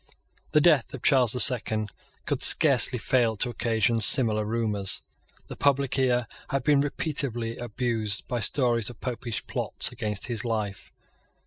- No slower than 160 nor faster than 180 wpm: No, average, 145 wpm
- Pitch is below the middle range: Yes, low, 120 Hz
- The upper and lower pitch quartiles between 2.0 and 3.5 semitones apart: Yes, average, 3.0 semitones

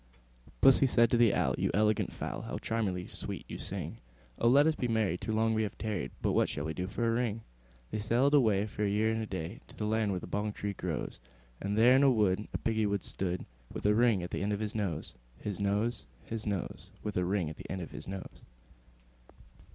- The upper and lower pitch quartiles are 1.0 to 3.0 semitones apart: Yes, narrow, 2.6 semitones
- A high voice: No, low, 105 Hz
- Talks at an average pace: No, fast, 245 wpm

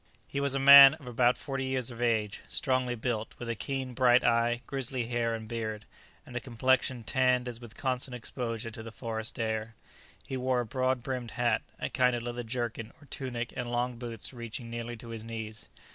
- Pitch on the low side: Yes, low, 120 Hz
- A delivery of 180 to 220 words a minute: Yes, fast, 205 wpm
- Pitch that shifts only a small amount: Yes, narrow, 2.0 semitones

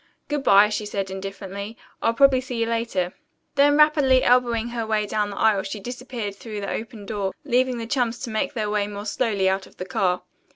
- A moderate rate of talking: No, fast, 210 wpm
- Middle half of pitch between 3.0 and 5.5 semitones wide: Yes, average, 3.6 semitones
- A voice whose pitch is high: Yes, high, 220 Hz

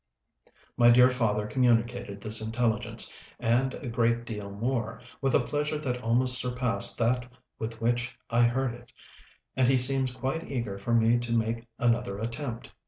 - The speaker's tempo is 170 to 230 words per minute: No, average, 160 wpm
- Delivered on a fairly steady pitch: Yes, narrow, 1.8 semitones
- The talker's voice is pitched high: No, low, 120 Hz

